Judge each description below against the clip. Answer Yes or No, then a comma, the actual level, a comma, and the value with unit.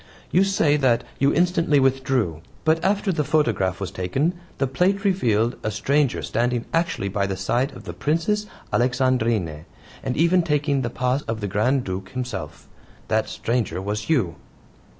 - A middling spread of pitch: No, wide, 6.4 semitones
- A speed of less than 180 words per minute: Yes, average, 160 wpm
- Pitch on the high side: No, low, 130 Hz